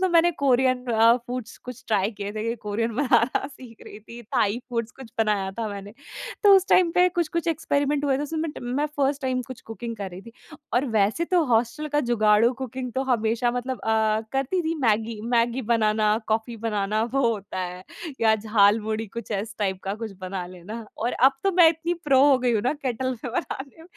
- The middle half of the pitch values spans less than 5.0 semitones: Yes, average, 3.8 semitones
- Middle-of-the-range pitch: No, high, 235 Hz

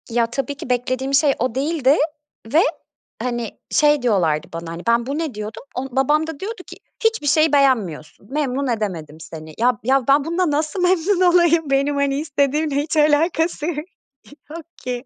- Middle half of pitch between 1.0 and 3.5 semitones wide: No, average, 4.4 semitones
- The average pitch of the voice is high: Yes, very high, 275 Hz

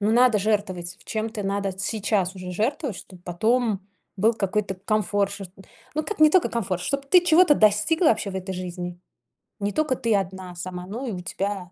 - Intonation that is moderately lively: Yes, average, 3.7 semitones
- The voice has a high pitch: Yes, high, 205 Hz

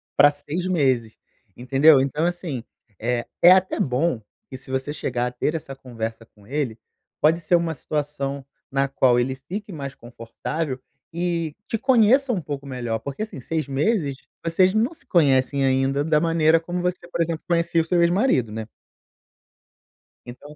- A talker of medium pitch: Yes, medium, 145 Hz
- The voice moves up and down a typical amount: Yes, average, 4.6 semitones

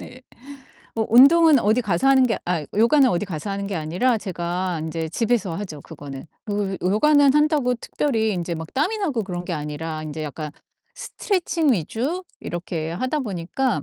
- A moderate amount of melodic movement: No, wide, 7.6 semitones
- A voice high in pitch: Yes, high, 200 Hz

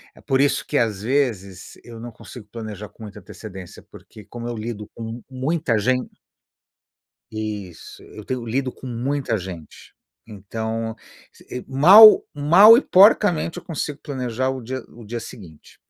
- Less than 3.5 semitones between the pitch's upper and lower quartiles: No, average, 3.9 semitones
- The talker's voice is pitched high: No, low, 120 Hz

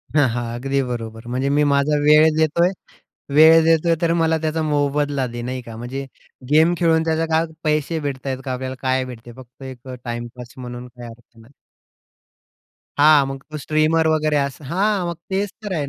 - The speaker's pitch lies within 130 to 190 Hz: Yes, medium, 140 Hz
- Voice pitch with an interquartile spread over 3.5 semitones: Yes, average, 4.0 semitones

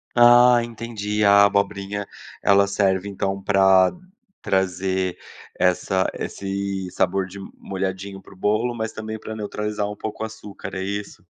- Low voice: Yes, low, 100 Hz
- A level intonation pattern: Yes, narrow, 1.8 semitones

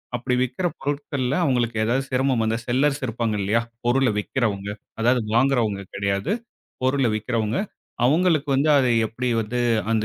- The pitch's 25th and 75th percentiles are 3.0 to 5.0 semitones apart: Yes, average, 3.4 semitones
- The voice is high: No, low, 125 Hz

